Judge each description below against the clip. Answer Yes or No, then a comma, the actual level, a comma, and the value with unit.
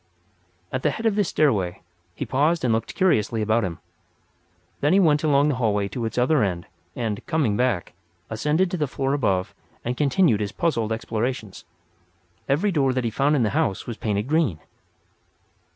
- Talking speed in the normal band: Yes, average, 185 wpm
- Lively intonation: Yes, wide, 5.7 semitones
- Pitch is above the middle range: No, low, 125 Hz